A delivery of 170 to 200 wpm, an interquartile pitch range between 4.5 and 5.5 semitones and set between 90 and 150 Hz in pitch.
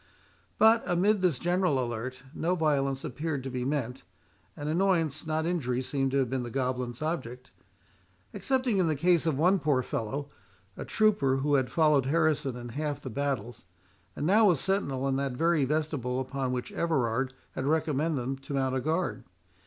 No: average, 175 wpm; average, 4.0 semitones; medium, 140 Hz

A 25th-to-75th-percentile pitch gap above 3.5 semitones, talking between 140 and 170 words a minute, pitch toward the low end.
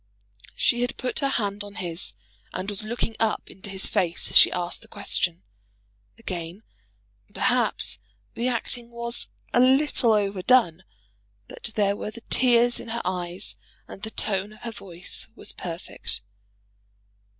No: average, 4.1 semitones; average, 150 wpm; high, 210 Hz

